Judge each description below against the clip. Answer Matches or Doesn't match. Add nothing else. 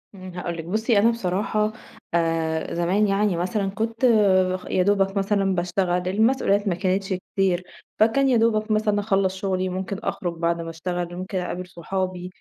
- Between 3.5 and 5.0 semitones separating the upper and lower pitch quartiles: Doesn't match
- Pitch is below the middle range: Doesn't match